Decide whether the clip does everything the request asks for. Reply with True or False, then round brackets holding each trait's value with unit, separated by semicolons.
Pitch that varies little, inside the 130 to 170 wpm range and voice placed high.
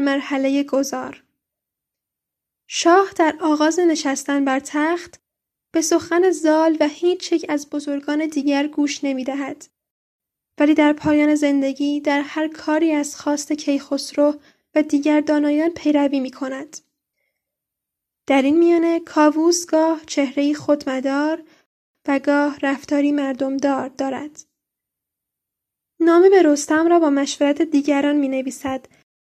False (2.1 semitones; 115 wpm; 295 Hz)